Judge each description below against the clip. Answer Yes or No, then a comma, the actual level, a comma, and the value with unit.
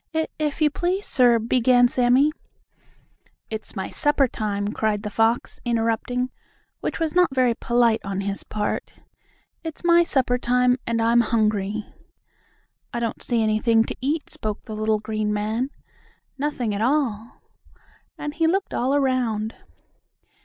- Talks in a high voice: Yes, high, 235 Hz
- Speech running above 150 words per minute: No, average, 145 wpm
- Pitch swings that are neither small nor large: Yes, average, 3.8 semitones